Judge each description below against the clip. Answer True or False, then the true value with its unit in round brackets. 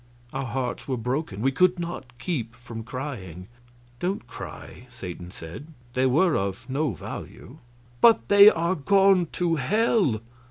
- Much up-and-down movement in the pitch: True (6.8 semitones)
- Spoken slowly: False (145 wpm)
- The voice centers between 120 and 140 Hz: True (135 Hz)